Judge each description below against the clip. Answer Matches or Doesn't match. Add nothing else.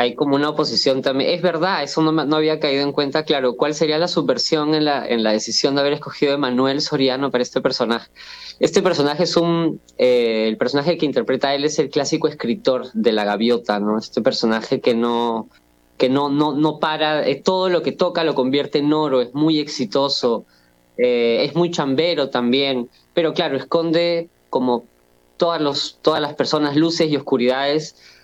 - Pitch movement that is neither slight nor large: Matches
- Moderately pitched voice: Matches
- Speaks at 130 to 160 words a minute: Doesn't match